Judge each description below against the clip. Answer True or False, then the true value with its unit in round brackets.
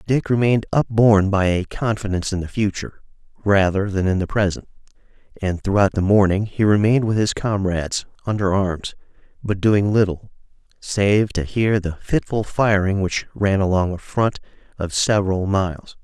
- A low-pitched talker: True (100 Hz)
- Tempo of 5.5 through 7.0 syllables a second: False (5.1 syllables/s)